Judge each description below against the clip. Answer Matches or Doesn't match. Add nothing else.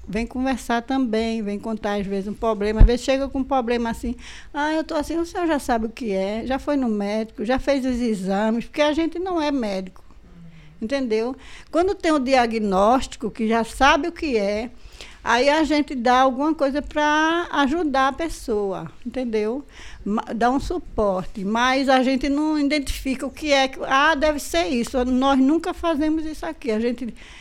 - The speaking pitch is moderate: Doesn't match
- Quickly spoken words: Matches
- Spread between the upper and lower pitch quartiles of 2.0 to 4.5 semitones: Doesn't match